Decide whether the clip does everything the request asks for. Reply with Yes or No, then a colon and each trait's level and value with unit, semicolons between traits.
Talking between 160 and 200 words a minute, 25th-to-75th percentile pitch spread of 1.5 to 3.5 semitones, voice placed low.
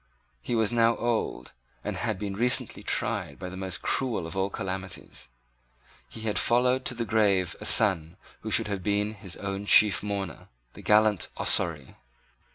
Yes: average, 165 wpm; average, 2.9 semitones; low, 100 Hz